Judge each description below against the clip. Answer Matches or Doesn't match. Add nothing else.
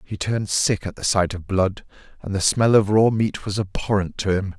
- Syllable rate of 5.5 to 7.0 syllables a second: Doesn't match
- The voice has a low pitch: Matches